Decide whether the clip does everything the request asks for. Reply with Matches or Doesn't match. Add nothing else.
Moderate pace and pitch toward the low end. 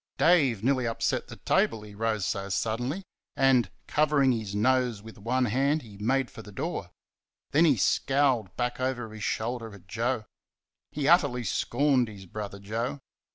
Matches